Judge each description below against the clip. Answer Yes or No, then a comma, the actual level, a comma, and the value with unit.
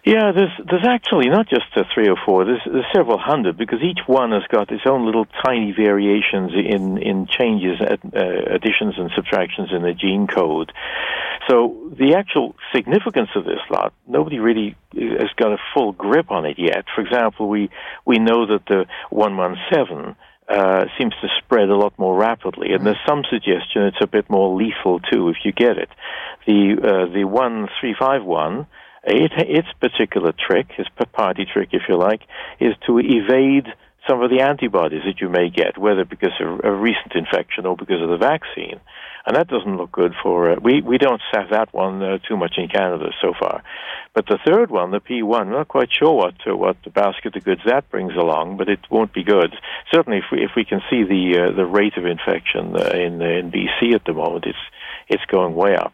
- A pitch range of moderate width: Yes, average, 4.2 semitones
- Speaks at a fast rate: Yes, fast, 210 wpm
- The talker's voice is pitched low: Yes, low, 105 Hz